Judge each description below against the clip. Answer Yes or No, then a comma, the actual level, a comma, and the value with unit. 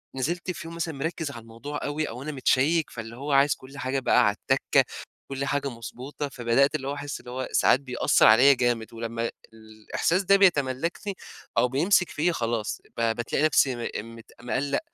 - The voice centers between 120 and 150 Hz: Yes, low, 135 Hz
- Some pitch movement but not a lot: Yes, average, 3.9 semitones